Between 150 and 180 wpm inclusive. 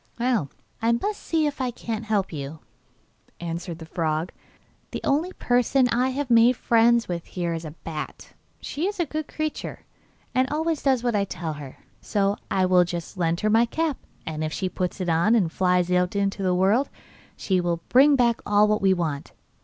No: average, 190 wpm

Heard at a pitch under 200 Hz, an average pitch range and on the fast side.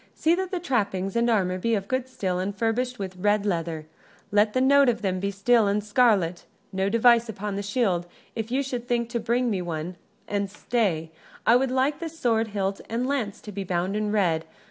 No: high, 210 Hz; average, 4.0 semitones; fast, 215 wpm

